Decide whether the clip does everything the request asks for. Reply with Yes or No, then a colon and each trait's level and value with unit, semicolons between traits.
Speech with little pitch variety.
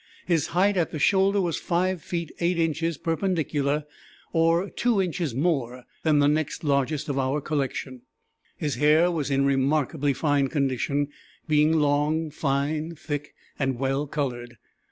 No: average, 3.1 semitones